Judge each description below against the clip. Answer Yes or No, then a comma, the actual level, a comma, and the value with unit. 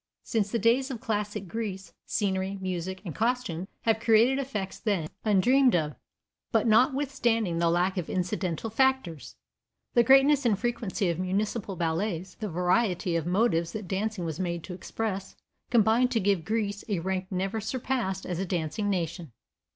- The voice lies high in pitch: Yes, high, 200 Hz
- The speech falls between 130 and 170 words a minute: Yes, average, 160 wpm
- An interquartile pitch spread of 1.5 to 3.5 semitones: No, average, 4.2 semitones